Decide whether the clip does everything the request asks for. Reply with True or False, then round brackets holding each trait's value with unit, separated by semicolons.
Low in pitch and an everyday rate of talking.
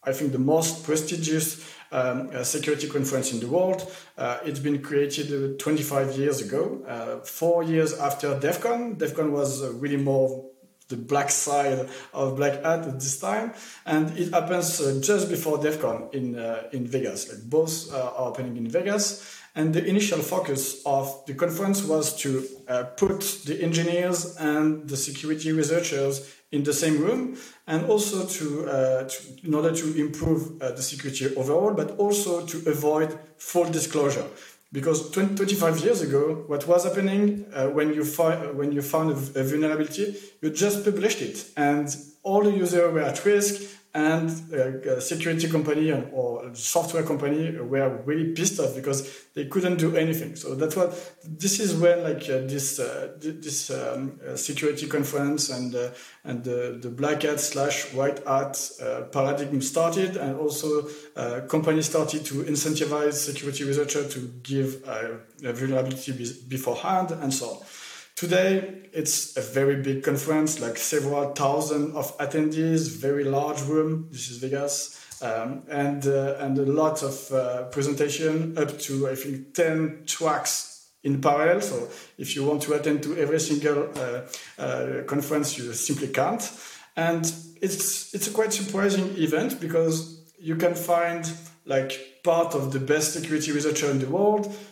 False (150 Hz; 165 wpm)